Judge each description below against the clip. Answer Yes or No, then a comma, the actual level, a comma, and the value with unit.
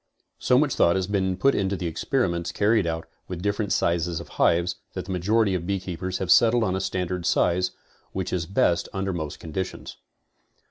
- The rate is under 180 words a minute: No, average, 195 wpm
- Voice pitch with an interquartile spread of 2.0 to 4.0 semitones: Yes, narrow, 2.6 semitones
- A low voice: Yes, very low, 95 Hz